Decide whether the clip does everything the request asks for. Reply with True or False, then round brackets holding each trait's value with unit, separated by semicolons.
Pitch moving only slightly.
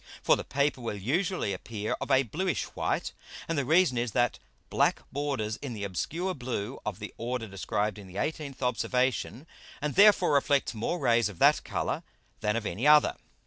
False (5.6 semitones)